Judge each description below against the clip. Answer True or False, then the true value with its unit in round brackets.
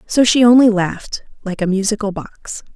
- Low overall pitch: False (210 Hz)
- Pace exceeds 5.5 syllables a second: False (5.1 syllables/s)